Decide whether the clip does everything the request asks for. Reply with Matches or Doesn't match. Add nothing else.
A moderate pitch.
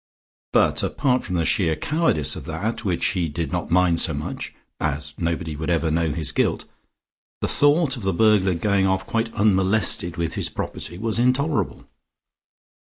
Doesn't match